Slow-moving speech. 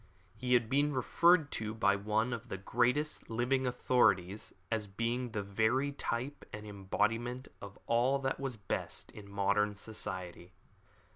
No: average, 145 wpm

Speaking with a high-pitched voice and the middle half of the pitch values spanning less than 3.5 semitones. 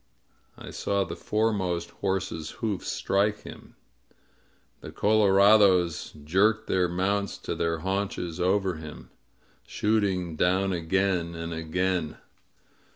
No: very low, 95 Hz; average, 2.9 semitones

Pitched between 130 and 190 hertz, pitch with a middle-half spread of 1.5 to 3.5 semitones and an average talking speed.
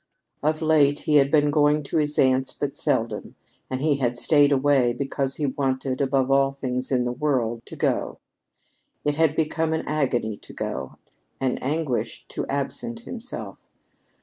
Yes: medium, 140 Hz; narrow, 2.5 semitones; average, 165 wpm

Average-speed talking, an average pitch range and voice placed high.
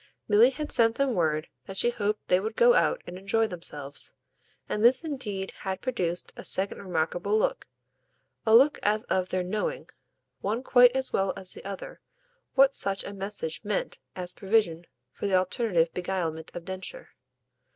Yes: average, 170 wpm; average, 4.2 semitones; high, 200 Hz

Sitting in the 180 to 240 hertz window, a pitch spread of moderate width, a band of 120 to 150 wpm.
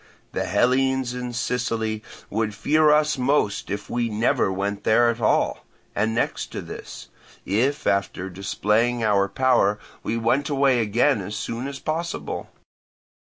No: low, 115 Hz; average, 4.2 semitones; average, 145 wpm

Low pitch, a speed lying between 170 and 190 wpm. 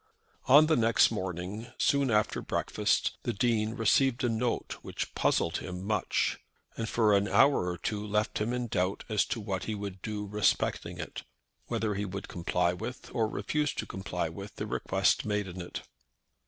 Yes: low, 105 Hz; average, 180 wpm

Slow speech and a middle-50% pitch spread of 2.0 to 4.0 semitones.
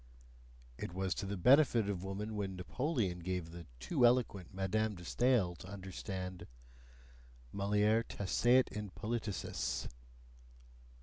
Yes: slow, 120 wpm; average, 3.3 semitones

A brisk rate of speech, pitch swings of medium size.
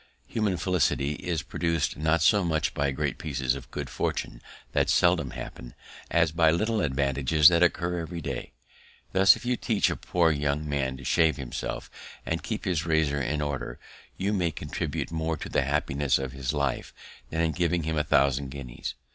No: average, 180 wpm; average, 3.4 semitones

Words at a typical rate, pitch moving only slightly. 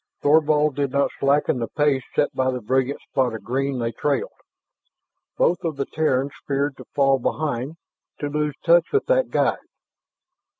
Yes: average, 165 wpm; narrow, 2.3 semitones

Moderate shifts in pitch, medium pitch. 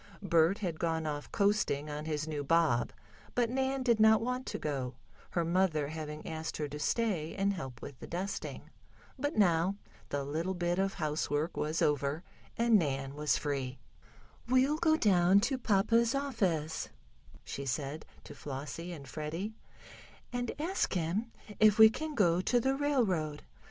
No: wide, 6.6 semitones; medium, 170 Hz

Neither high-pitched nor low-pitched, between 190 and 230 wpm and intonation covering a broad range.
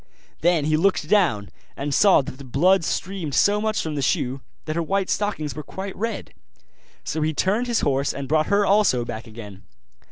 Yes: medium, 155 Hz; average, 195 wpm; wide, 6.2 semitones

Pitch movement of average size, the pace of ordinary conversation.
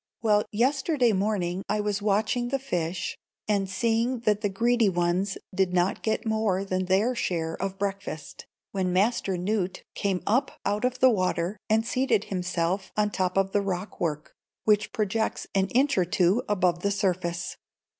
Yes: average, 3.0 semitones; average, 170 wpm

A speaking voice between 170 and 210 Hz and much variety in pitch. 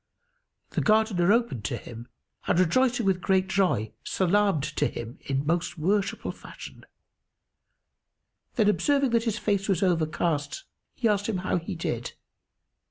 No: high, 190 Hz; average, 4.5 semitones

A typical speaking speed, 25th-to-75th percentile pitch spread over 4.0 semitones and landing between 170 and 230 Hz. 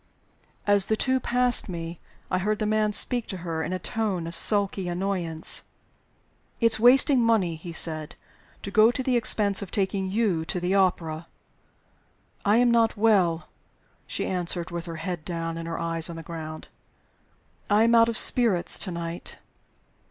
Yes: average, 170 wpm; average, 4.6 semitones; high, 190 Hz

